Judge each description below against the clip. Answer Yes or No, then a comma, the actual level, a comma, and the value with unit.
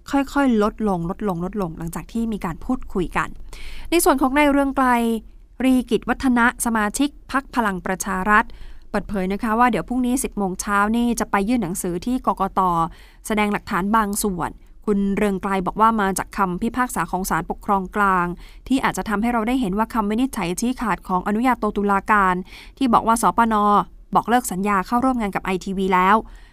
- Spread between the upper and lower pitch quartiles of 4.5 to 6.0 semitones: No, average, 4.0 semitones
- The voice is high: Yes, high, 210 Hz